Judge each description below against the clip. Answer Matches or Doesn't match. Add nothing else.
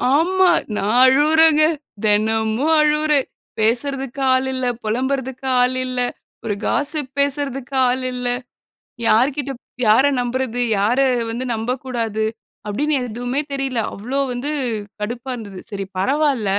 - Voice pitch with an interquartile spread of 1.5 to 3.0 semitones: Doesn't match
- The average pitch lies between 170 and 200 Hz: Doesn't match